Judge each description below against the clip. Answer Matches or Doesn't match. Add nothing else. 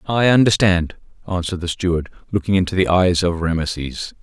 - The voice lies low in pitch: Matches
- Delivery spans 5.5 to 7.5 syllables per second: Matches